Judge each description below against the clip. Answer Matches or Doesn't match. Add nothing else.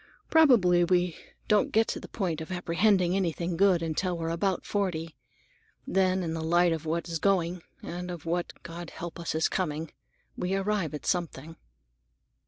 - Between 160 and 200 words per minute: Matches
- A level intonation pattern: Matches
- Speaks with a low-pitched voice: Doesn't match